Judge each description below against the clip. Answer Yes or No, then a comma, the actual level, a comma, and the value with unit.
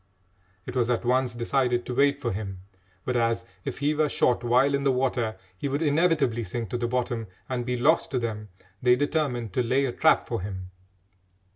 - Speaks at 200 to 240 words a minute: Yes, fast, 205 wpm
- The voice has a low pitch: Yes, low, 125 Hz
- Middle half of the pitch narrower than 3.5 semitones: Yes, average, 2.9 semitones